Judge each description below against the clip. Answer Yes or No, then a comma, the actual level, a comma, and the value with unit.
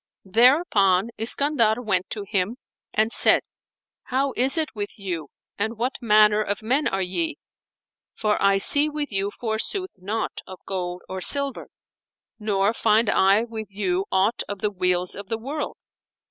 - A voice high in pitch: Yes, high, 215 Hz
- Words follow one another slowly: No, average, 155 wpm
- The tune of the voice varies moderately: Yes, average, 4.0 semitones